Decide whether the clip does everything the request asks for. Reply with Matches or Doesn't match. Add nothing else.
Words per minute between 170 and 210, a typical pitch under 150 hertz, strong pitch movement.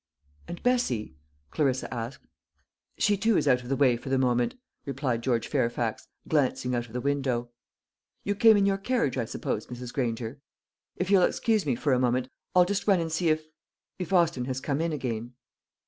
Matches